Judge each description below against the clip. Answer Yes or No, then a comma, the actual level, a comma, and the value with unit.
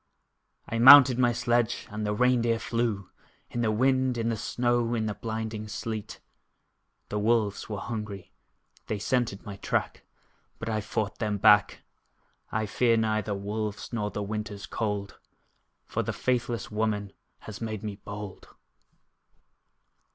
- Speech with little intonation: Yes, narrow, 2.2 semitones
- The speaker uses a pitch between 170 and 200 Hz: No, low, 110 Hz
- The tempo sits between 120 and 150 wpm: Yes, average, 145 wpm